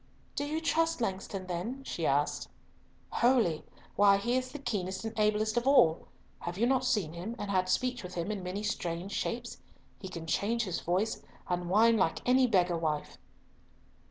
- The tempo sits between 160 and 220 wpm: Yes, average, 180 wpm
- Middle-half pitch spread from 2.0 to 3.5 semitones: No, average, 5.1 semitones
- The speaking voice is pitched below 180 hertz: No, high, 205 Hz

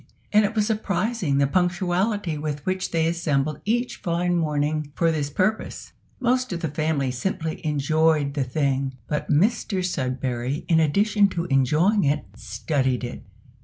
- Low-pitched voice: No, medium, 160 Hz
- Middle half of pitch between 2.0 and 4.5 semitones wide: No, average, 4.9 semitones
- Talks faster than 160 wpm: No, average, 150 wpm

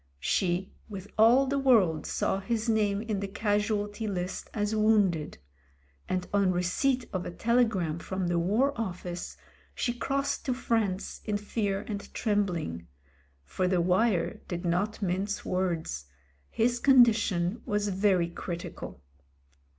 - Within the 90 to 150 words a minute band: Yes, average, 140 wpm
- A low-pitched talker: No, high, 200 Hz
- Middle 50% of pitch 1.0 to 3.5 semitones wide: No, average, 3.9 semitones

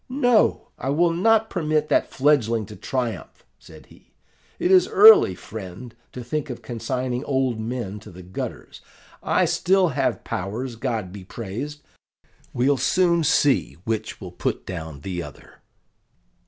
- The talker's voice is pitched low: Yes, low, 125 Hz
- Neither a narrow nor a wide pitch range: No, wide, 6.6 semitones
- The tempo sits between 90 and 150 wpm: Yes, average, 145 wpm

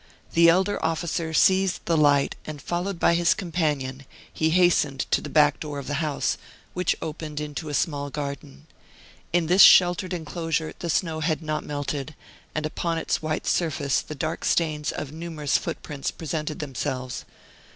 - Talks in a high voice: No, medium, 155 Hz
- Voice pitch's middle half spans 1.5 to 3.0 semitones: Yes, narrow, 2.5 semitones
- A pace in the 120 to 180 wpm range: Yes, average, 160 wpm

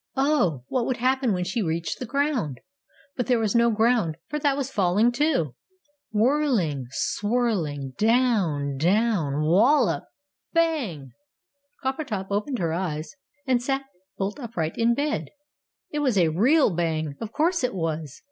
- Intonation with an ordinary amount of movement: No, wide, 8.1 semitones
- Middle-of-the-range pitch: No, high, 220 Hz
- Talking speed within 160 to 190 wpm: No, average, 145 wpm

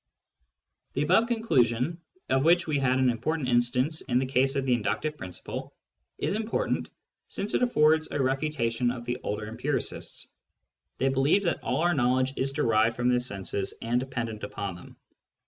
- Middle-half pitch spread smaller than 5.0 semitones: Yes, average, 4.3 semitones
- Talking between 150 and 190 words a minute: Yes, average, 165 wpm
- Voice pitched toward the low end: Yes, low, 130 Hz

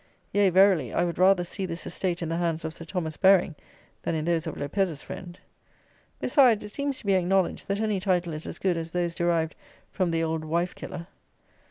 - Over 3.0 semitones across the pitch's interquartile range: No, average, 2.7 semitones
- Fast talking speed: Yes, fast, 210 wpm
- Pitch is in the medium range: Yes, medium, 175 Hz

